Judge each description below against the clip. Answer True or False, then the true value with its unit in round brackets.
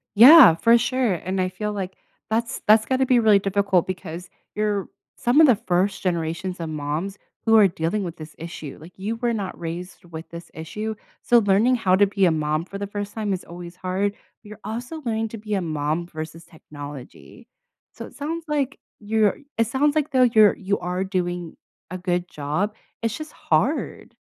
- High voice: True (195 Hz)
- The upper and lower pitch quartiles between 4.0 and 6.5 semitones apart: True (4.3 semitones)